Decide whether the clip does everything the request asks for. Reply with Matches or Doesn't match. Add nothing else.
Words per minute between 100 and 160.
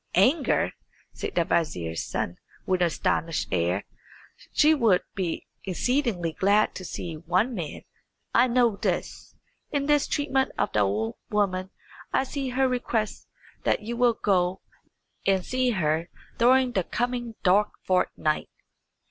Matches